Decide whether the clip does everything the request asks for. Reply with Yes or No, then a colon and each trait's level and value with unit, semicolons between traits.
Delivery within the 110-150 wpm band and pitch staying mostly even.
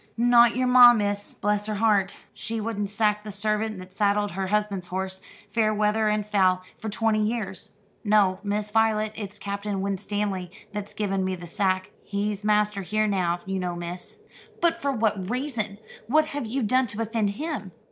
No: average, 175 wpm; narrow, 2.2 semitones